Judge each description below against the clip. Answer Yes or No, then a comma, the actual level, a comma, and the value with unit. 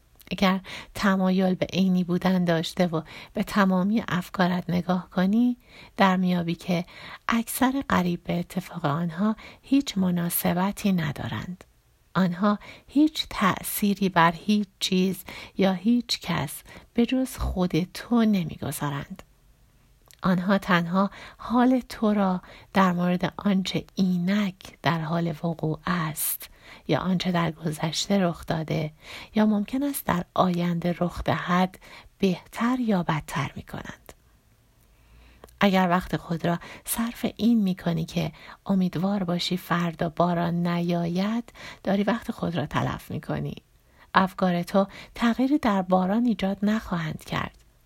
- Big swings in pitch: No, average, 3.0 semitones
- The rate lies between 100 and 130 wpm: Yes, average, 125 wpm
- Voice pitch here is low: No, medium, 180 Hz